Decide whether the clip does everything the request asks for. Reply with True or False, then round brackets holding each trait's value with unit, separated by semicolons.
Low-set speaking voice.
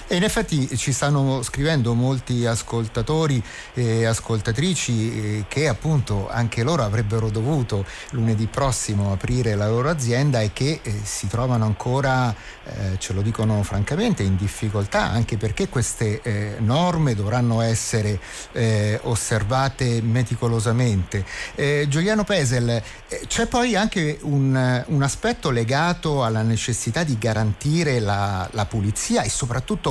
True (120 Hz)